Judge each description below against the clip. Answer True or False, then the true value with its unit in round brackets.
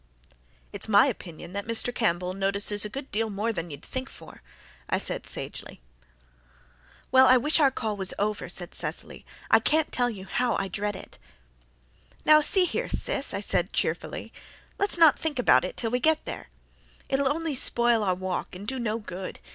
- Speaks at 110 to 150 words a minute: False (185 wpm)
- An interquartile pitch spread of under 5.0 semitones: False (5.3 semitones)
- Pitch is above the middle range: True (225 Hz)